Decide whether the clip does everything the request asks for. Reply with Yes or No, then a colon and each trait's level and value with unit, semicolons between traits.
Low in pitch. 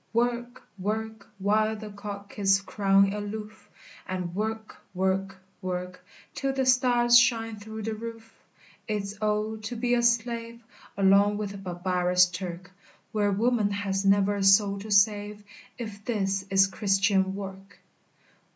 No: high, 205 Hz